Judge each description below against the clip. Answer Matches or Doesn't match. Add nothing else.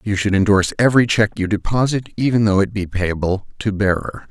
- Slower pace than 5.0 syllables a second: Doesn't match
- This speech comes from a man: Matches